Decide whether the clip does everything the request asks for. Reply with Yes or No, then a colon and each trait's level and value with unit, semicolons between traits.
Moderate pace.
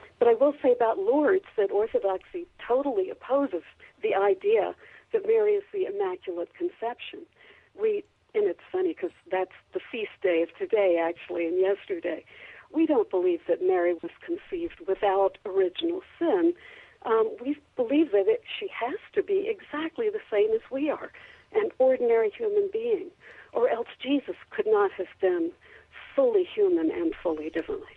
Yes: average, 155 wpm